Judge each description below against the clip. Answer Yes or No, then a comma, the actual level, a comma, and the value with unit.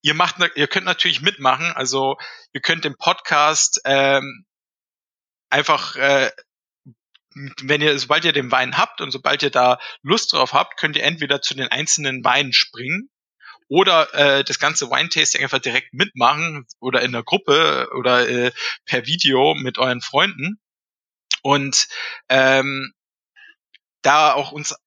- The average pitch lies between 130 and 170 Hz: Yes, medium, 140 Hz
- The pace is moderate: Yes, average, 145 wpm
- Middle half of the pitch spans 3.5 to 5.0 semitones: No, narrow, 2.6 semitones